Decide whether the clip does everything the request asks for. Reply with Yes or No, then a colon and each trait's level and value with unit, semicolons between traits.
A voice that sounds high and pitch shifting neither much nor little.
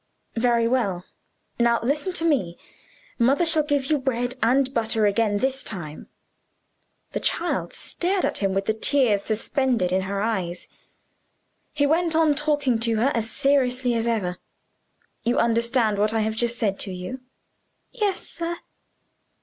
Yes: high, 235 Hz; average, 4.6 semitones